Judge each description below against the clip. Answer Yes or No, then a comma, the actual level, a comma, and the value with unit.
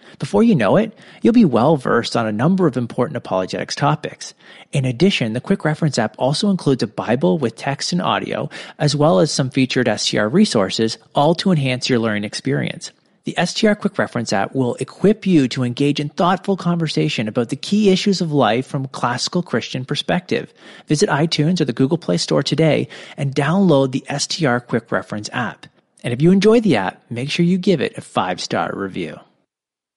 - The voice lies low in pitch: No, medium, 145 Hz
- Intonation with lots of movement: Yes, wide, 6.7 semitones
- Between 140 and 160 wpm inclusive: No, average, 190 wpm